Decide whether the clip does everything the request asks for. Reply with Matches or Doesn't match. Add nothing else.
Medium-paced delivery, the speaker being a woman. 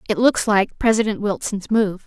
Matches